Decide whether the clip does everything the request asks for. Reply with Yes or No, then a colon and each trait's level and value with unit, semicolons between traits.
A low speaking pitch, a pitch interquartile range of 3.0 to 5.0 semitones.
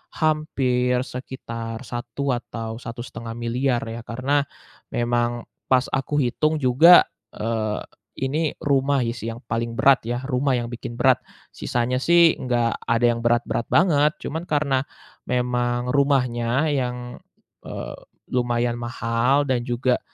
No: low, 125 Hz; narrow, 2.6 semitones